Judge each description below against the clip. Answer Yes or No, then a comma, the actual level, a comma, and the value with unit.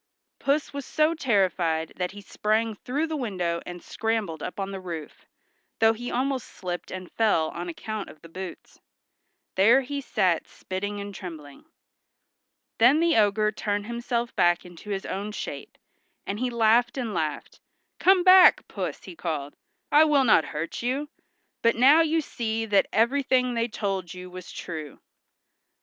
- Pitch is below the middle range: No, high, 215 Hz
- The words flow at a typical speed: Yes, average, 160 wpm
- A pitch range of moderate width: No, wide, 5.7 semitones